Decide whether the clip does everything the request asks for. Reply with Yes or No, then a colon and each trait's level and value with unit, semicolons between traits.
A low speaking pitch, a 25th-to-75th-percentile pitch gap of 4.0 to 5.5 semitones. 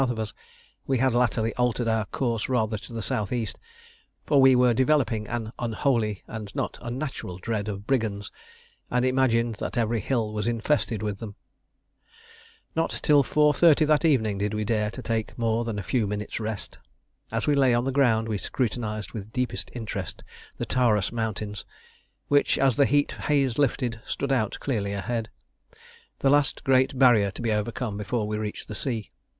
No: low, 115 Hz; average, 3.4 semitones